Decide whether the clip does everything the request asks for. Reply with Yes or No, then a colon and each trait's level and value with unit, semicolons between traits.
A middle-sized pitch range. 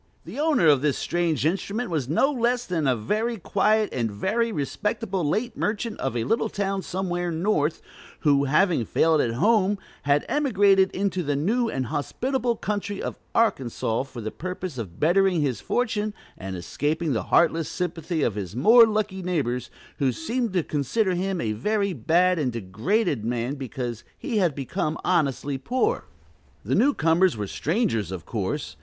No: wide, 7.5 semitones